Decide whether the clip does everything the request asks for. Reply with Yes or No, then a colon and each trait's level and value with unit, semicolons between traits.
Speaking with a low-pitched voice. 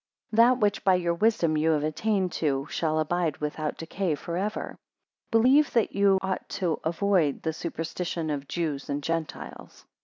No: medium, 170 Hz